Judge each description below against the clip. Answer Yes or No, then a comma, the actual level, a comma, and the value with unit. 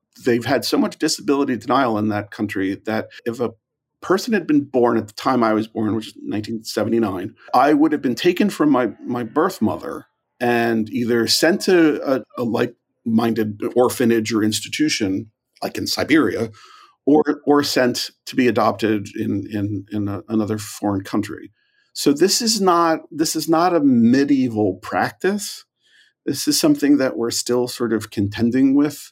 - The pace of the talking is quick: No, average, 165 wpm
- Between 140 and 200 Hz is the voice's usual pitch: No, low, 125 Hz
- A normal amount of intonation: No, wide, 6.0 semitones